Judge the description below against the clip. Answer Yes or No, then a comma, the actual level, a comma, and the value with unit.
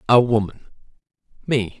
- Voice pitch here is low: Yes, low, 115 Hz